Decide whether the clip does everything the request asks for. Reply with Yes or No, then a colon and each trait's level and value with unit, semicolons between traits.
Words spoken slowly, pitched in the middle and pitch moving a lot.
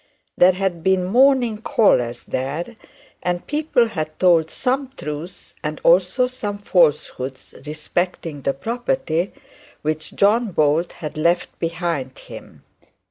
Yes: slow, 120 wpm; medium, 175 Hz; wide, 5.7 semitones